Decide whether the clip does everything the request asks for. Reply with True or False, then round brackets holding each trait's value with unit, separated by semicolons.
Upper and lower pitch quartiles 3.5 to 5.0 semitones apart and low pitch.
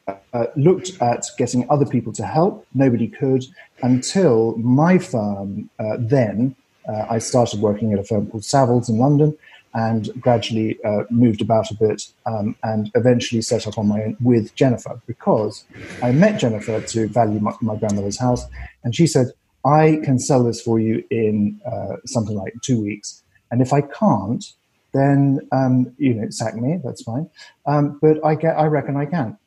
True (3.8 semitones; 120 Hz)